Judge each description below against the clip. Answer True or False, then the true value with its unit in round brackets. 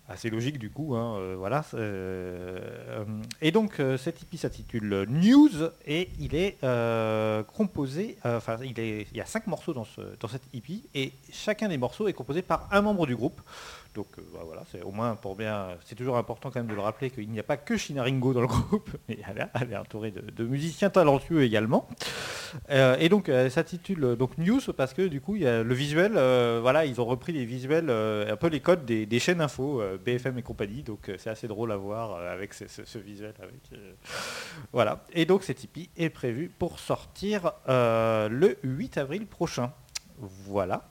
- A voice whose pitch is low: True (130 Hz)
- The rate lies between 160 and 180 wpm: False (210 wpm)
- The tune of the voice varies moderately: False (6.7 semitones)